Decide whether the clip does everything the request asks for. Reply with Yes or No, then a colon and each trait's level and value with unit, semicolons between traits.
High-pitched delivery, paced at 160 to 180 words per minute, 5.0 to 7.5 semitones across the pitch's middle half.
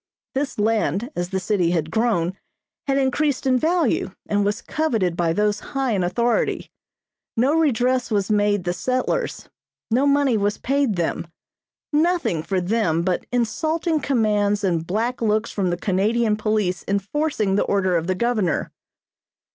No: high, 215 Hz; average, 150 wpm; average, 5.3 semitones